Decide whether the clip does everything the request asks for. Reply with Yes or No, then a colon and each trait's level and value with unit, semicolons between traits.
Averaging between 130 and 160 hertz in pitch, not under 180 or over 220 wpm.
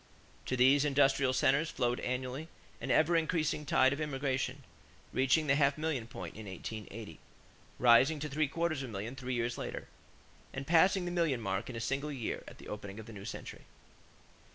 Yes: low, 135 Hz; average, 185 wpm